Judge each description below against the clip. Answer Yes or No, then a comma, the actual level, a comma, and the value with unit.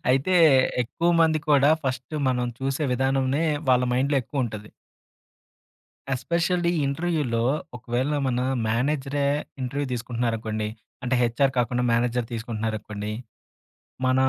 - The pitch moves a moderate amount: Yes, average, 3.3 semitones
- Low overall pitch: Yes, low, 130 Hz